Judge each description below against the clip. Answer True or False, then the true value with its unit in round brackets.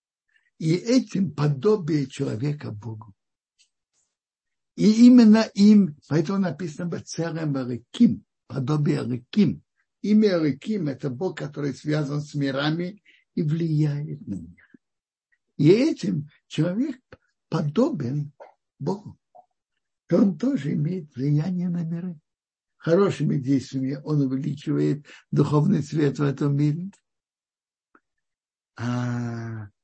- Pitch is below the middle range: False (155 Hz)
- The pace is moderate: False (90 wpm)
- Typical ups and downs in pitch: False (5.7 semitones)